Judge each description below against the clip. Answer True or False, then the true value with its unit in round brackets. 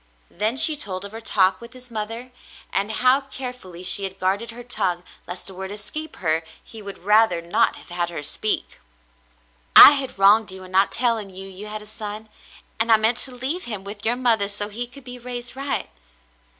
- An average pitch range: True (4.1 semitones)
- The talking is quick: True (210 wpm)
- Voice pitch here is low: False (215 Hz)